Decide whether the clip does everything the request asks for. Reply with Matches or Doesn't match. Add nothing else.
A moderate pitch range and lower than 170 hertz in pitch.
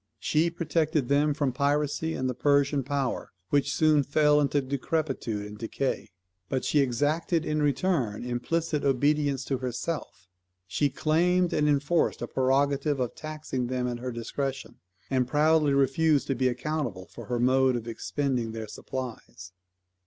Matches